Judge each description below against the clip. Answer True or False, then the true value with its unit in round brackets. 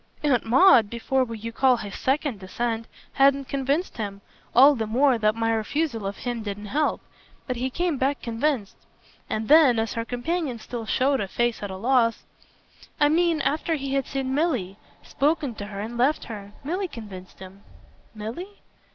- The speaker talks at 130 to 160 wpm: False (175 wpm)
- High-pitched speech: True (245 Hz)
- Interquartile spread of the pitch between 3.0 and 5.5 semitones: True (4.3 semitones)